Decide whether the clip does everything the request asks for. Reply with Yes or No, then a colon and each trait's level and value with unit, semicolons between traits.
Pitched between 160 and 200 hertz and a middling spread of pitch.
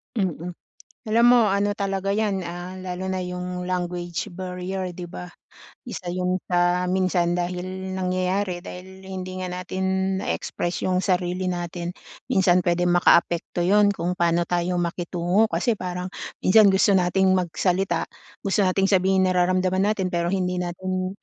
No: medium, 185 Hz; narrow, 1.2 semitones